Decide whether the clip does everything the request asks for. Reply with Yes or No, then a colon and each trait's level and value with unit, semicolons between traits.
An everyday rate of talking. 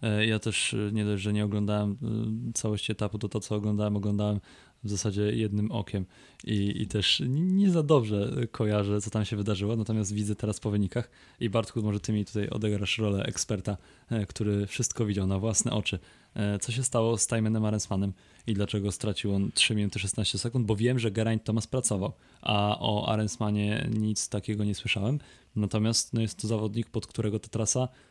No: fast, 180 wpm